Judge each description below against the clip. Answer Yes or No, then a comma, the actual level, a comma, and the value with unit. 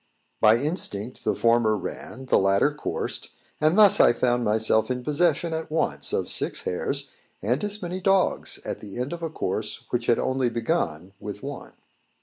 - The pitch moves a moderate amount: No, wide, 6.5 semitones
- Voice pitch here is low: Yes, low, 125 Hz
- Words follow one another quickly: No, average, 175 wpm